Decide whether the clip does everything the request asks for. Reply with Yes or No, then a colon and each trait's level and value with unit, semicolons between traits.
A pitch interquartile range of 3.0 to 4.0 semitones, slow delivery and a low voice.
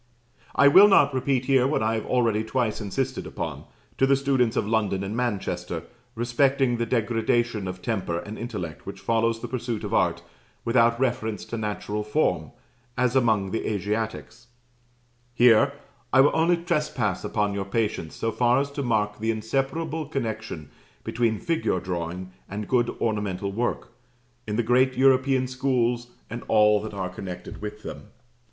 No: average, 3.6 semitones; average, 160 wpm; low, 115 Hz